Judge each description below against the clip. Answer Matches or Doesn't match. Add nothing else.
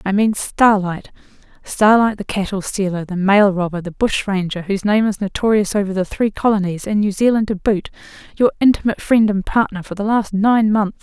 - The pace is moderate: Matches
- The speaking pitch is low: Doesn't match